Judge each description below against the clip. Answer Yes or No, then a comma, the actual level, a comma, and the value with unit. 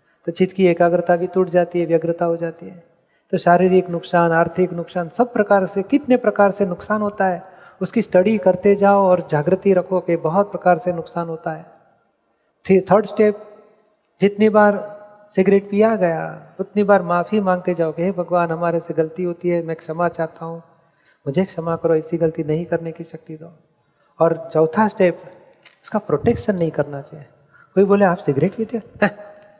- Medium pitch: Yes, medium, 175 Hz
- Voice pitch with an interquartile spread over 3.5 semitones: No, average, 3.2 semitones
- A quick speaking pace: Yes, fast, 180 wpm